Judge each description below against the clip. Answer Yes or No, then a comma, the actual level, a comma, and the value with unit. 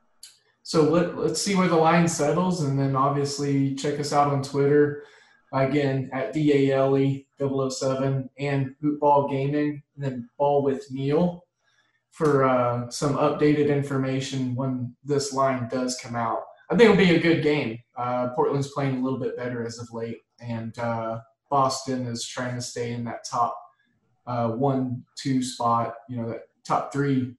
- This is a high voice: No, low, 135 Hz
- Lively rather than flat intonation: No, average, 2.8 semitones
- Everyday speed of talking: Yes, average, 160 wpm